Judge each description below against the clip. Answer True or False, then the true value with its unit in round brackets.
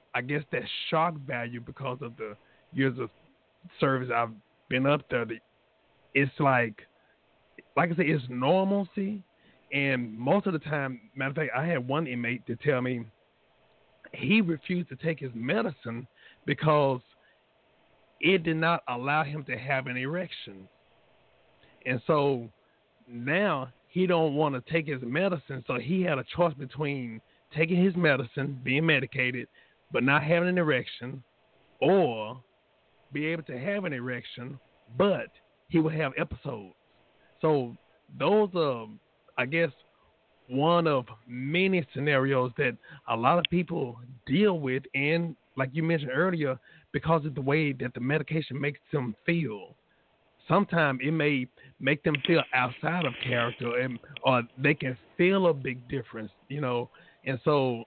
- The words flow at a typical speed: True (150 wpm)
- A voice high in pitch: False (140 Hz)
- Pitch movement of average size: True (4.6 semitones)